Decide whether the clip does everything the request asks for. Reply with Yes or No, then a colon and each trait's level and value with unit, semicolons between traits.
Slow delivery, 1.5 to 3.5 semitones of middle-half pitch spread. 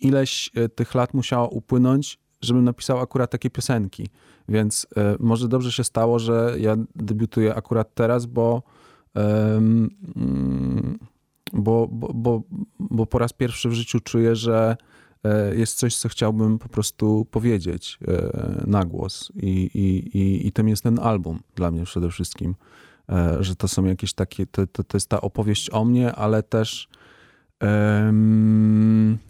No: average, 155 wpm; narrow, 2.5 semitones